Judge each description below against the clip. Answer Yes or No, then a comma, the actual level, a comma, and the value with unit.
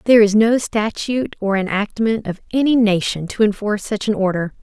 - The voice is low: No, high, 210 Hz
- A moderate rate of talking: Yes, average, 180 wpm